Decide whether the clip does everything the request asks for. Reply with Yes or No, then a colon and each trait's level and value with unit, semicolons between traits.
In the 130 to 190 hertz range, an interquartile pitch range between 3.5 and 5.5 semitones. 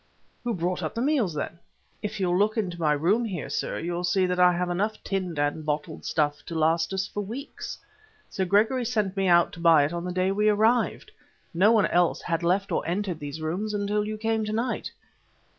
Yes: medium, 185 Hz; average, 3.8 semitones